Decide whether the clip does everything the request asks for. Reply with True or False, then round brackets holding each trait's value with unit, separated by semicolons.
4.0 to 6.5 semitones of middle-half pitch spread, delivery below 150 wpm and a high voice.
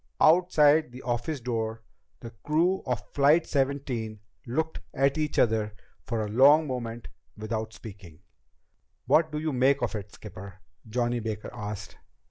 False (5.1 semitones; 140 wpm; 120 Hz)